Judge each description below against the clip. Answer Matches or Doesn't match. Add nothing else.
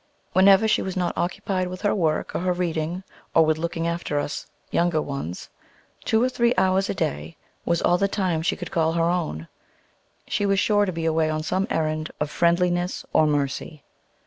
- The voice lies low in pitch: Doesn't match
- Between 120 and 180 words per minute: Doesn't match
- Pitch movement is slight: Doesn't match